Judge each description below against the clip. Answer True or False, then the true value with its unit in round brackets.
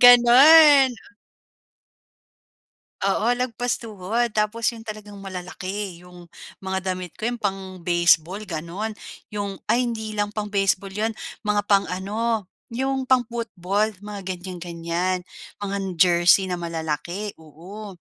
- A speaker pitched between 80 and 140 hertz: False (200 Hz)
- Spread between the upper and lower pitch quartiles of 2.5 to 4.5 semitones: True (3.5 semitones)